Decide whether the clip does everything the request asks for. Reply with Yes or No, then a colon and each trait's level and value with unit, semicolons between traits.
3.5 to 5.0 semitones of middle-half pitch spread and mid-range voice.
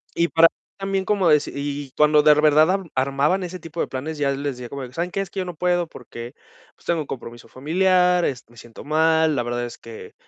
Yes: average, 4.5 semitones; medium, 150 Hz